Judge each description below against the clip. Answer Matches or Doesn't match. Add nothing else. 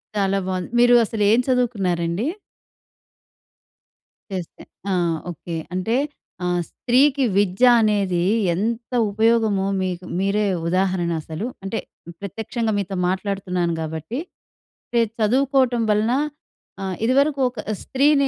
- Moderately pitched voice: Doesn't match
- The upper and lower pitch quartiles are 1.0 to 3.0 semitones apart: Doesn't match